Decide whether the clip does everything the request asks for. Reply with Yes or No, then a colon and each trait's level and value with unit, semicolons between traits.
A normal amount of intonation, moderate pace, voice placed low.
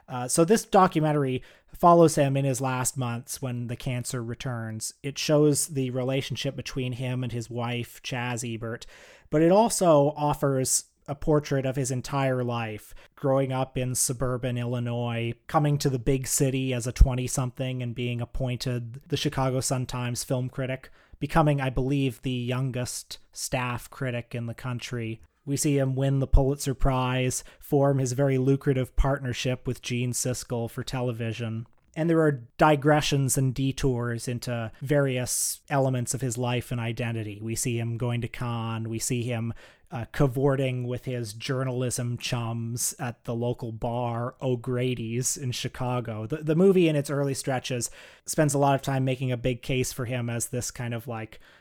No: narrow, 2.2 semitones; average, 165 wpm; low, 130 Hz